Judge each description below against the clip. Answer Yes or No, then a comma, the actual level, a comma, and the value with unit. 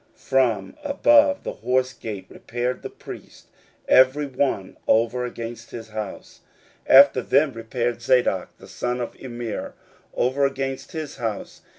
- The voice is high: No, low, 125 Hz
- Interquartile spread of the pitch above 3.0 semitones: No, average, 2.7 semitones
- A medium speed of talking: Yes, average, 145 wpm